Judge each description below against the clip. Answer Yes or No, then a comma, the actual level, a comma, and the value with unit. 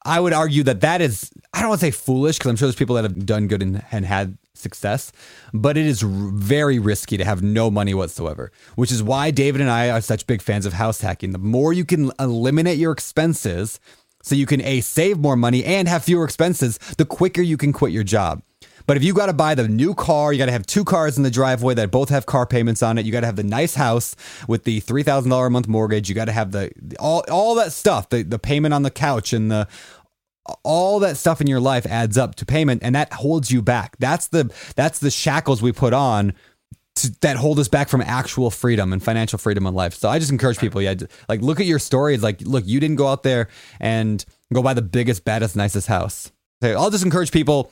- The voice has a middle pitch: No, low, 125 Hz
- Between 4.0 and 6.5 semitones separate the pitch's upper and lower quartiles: Yes, average, 4.9 semitones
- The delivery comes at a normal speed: No, fast, 250 wpm